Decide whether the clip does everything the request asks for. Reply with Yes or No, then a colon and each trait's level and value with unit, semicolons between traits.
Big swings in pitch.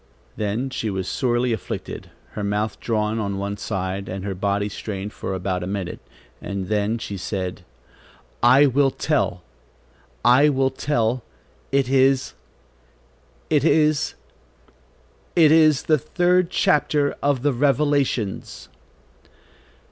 Yes: wide, 5.9 semitones